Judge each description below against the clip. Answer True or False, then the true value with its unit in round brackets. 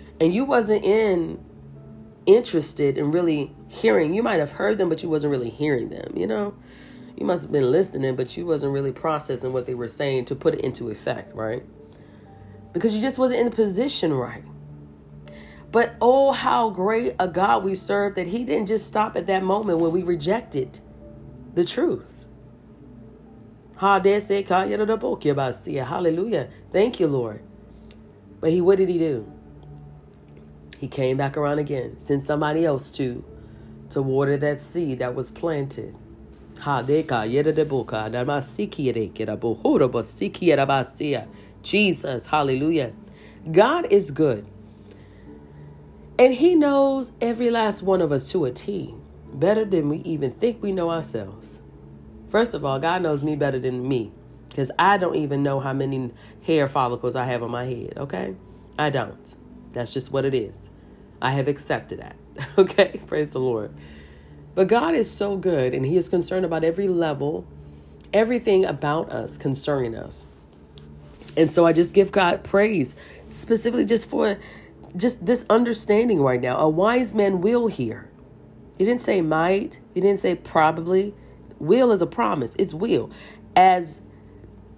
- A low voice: False (145 Hz)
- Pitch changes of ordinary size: False (8.9 semitones)